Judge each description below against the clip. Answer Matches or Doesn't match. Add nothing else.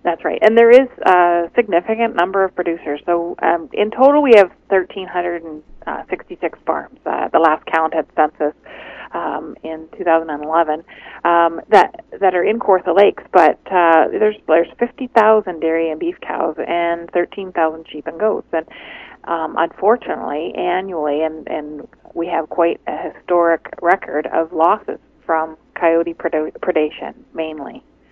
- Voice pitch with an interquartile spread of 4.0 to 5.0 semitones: Doesn't match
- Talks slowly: Doesn't match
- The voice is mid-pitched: Matches